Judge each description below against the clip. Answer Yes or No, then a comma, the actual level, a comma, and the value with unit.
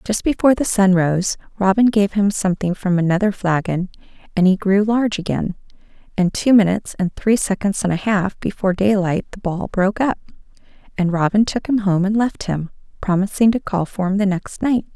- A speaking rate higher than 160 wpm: Yes, average, 195 wpm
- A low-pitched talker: No, high, 195 Hz